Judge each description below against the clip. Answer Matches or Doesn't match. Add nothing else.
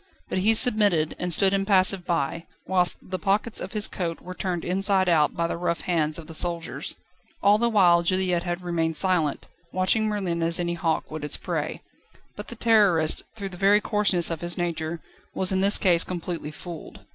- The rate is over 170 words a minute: Matches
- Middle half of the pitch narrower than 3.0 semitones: Matches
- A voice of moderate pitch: Matches